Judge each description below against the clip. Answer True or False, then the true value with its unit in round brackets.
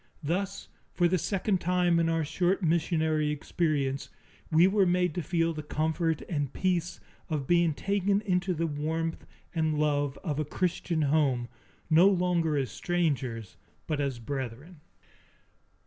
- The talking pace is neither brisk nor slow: True (145 wpm)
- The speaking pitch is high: False (165 Hz)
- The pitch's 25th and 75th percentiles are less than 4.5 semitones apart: True (3.2 semitones)